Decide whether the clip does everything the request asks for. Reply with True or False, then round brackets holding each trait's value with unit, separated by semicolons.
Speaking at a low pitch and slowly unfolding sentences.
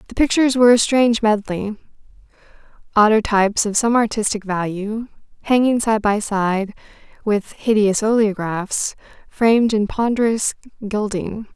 False (215 Hz; 110 wpm)